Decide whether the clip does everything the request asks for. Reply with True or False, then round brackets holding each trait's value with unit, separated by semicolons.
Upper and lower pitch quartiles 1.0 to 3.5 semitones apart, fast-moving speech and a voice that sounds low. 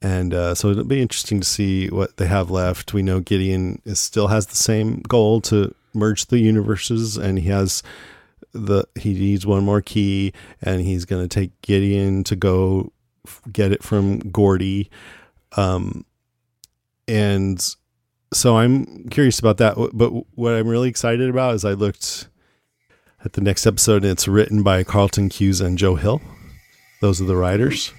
False (2.8 semitones; 170 wpm; 100 Hz)